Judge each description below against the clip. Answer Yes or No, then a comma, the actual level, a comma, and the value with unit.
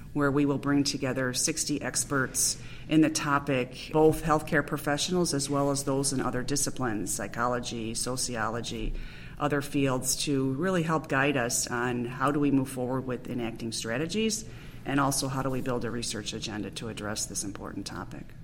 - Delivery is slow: No, average, 170 wpm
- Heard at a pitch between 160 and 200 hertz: No, low, 130 Hz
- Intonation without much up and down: No, average, 3.1 semitones